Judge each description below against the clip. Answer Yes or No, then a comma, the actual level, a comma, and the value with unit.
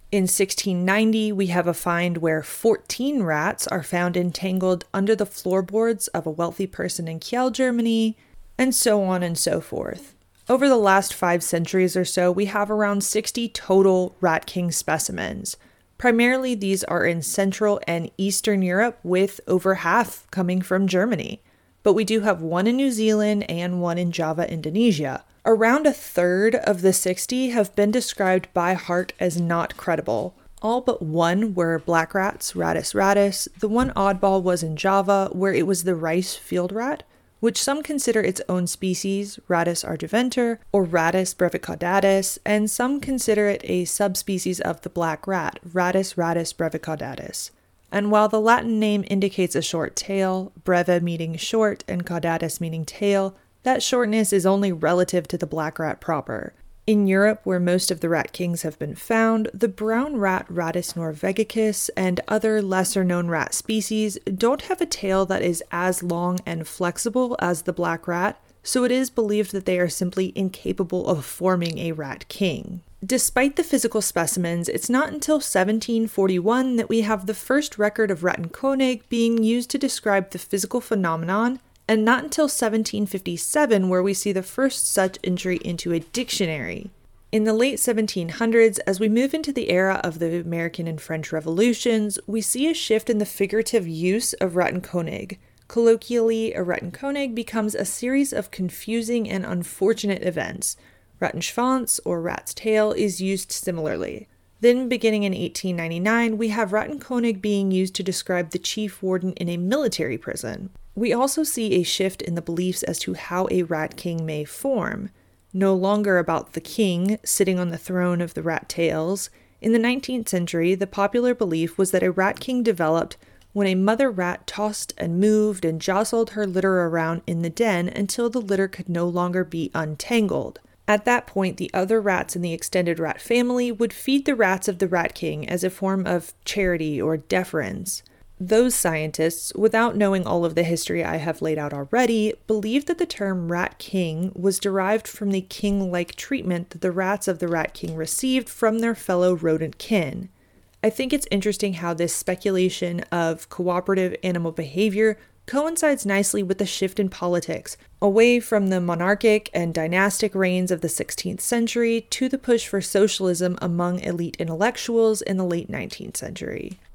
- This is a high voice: Yes, high, 195 Hz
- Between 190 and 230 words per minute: No, average, 170 wpm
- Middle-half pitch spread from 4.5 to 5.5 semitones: No, average, 3.9 semitones